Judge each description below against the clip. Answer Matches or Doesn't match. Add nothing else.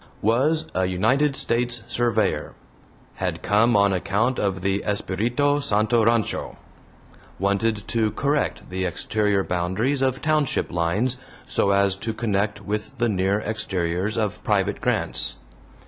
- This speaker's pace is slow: Matches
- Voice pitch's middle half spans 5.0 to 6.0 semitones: Doesn't match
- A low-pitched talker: Matches